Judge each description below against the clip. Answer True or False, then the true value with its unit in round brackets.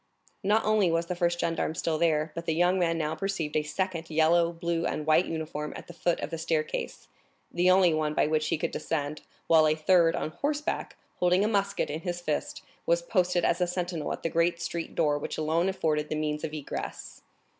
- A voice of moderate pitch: True (165 Hz)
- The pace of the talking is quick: True (215 wpm)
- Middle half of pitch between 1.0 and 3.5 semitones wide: True (2.4 semitones)